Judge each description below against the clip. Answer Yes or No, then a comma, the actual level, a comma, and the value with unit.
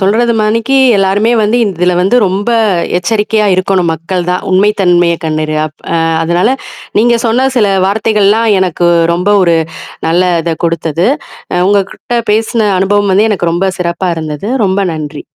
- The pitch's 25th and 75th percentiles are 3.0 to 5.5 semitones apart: Yes, average, 3.6 semitones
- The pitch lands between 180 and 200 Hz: Yes, high, 190 Hz